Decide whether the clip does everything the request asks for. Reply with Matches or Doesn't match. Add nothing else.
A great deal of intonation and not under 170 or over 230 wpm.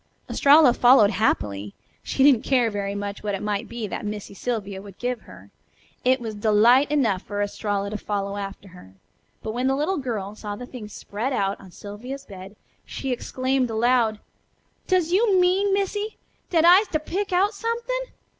Matches